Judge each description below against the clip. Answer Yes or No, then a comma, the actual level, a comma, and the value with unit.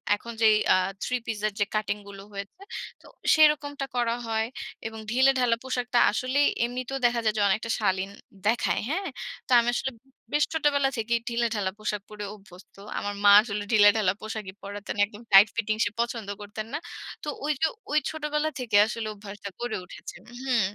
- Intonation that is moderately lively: Yes, average, 3.6 semitones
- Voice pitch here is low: No, high, 225 Hz